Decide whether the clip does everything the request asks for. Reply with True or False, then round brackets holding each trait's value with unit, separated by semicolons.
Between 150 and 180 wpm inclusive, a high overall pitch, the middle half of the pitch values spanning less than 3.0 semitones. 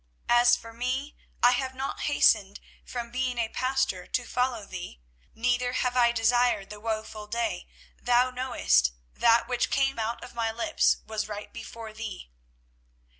True (160 wpm; 235 Hz; 2.4 semitones)